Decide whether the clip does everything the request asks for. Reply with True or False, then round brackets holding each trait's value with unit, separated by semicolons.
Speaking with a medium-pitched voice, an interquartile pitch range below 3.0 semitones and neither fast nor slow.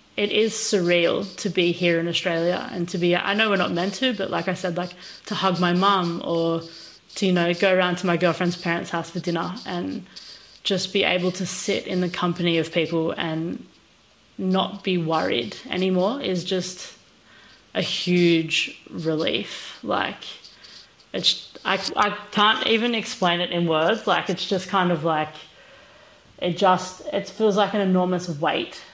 True (180 Hz; 2.4 semitones; 175 wpm)